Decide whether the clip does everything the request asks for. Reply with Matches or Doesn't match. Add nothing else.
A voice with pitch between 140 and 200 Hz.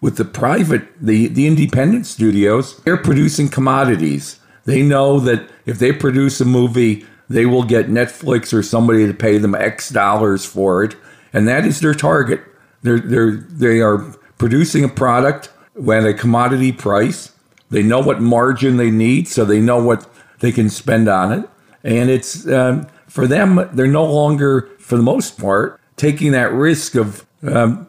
Doesn't match